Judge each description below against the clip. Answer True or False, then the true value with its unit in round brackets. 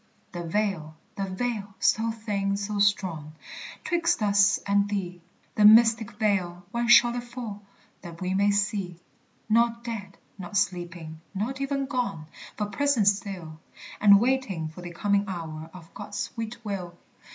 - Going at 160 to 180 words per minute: False (150 wpm)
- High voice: True (200 Hz)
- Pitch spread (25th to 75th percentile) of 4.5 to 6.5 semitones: False (3.9 semitones)